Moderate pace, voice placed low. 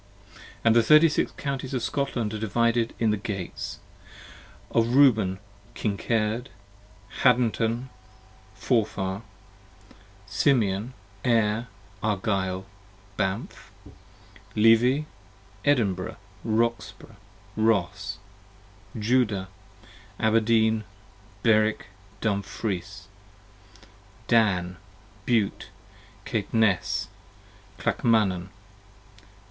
No: slow, 65 wpm; low, 110 Hz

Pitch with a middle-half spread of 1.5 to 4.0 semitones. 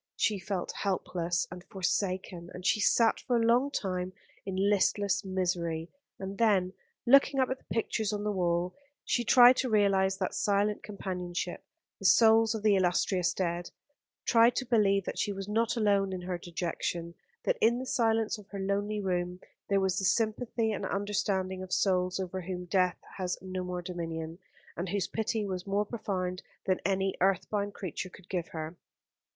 Yes: average, 2.8 semitones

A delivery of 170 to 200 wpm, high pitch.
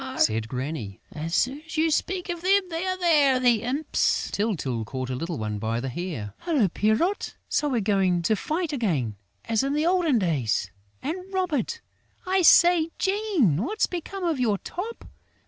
Yes: average, 175 wpm; very high, 255 Hz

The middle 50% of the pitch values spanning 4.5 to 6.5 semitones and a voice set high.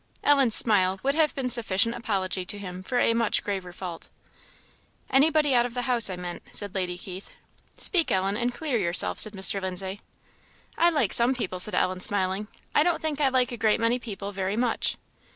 Yes: average, 4.9 semitones; high, 215 Hz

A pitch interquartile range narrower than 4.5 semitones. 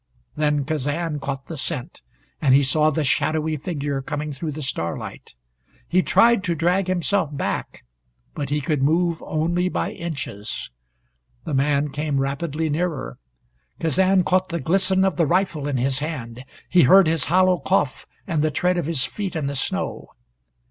Yes: average, 3.6 semitones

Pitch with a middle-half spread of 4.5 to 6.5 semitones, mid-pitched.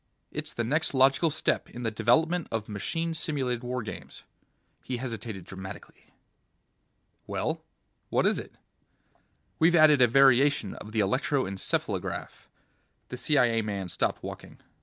No: average, 5.0 semitones; low, 125 Hz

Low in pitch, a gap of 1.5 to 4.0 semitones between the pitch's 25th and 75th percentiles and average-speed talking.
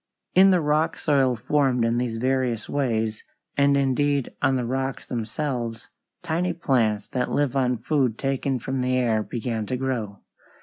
Yes: low, 130 Hz; average, 3.2 semitones; average, 160 wpm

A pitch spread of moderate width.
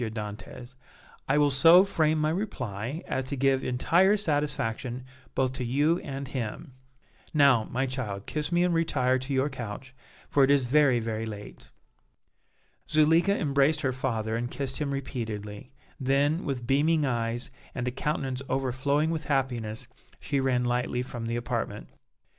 Yes: average, 3.3 semitones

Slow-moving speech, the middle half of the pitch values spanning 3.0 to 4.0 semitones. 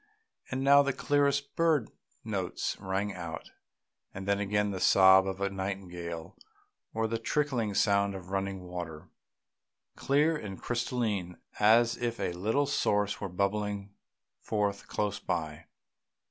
Yes: slow, 130 wpm; average, 3.5 semitones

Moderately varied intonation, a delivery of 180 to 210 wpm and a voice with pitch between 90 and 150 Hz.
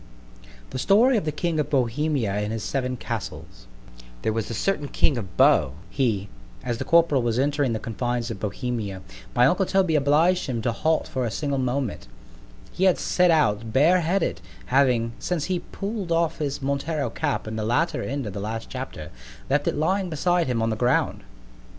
No: wide, 5.9 semitones; average, 190 wpm; low, 135 Hz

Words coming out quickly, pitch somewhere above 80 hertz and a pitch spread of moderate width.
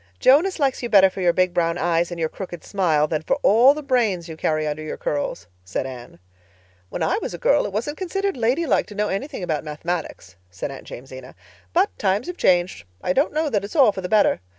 No: fast, 230 wpm; medium, 185 Hz; wide, 8.3 semitones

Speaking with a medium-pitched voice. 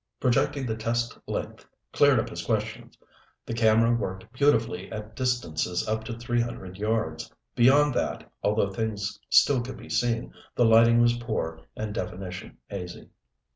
No: low, 115 Hz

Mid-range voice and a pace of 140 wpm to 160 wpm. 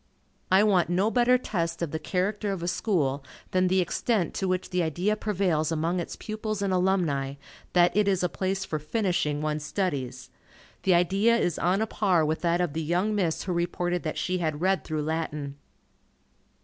No: medium, 180 Hz; average, 190 wpm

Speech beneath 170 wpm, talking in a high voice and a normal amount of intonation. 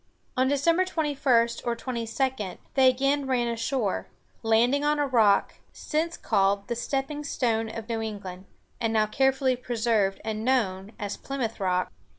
Yes: average, 150 wpm; high, 235 Hz; average, 3.7 semitones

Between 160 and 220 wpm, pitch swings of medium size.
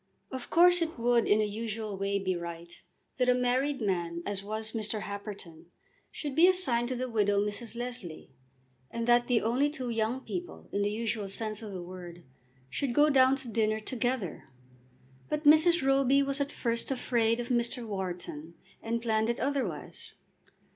Yes: average, 175 wpm; average, 4.2 semitones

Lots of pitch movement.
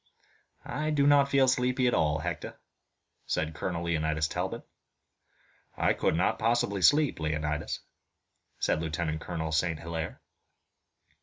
Yes: wide, 8.3 semitones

